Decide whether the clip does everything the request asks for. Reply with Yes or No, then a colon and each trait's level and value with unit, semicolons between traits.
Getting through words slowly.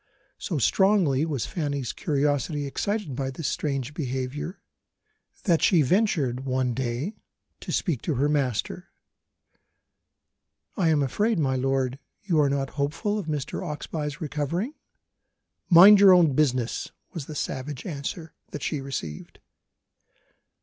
Yes: slow, 130 wpm